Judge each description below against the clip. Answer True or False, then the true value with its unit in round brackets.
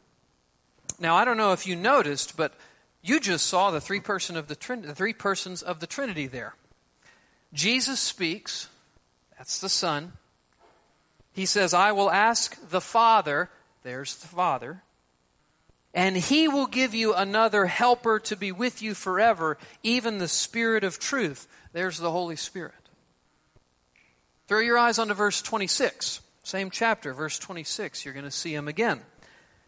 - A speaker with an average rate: True (155 wpm)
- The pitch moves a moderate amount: False (6.3 semitones)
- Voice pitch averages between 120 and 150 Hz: False (190 Hz)